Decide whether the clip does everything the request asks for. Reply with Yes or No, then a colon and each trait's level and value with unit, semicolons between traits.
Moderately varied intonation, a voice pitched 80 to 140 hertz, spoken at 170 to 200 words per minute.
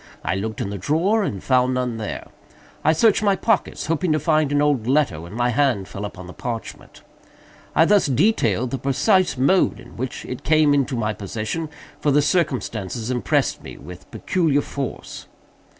No: wide, 5.7 semitones; low, 135 Hz; average, 180 wpm